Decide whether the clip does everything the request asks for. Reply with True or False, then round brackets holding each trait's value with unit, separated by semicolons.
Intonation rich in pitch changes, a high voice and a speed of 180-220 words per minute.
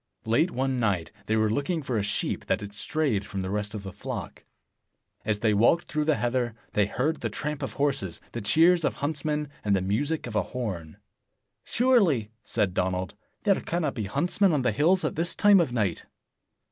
False (7.0 semitones; 120 Hz; 200 wpm)